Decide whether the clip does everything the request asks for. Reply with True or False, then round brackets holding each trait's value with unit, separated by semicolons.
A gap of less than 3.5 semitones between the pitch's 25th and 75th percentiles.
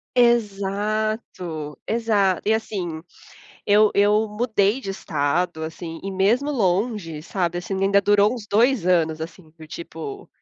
False (4.1 semitones)